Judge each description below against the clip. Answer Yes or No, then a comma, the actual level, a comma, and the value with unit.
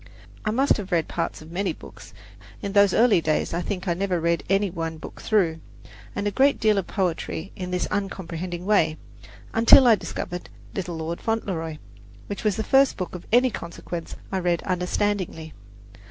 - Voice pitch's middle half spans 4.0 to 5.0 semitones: No, average, 3.4 semitones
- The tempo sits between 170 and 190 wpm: Yes, average, 180 wpm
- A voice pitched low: No, medium, 185 Hz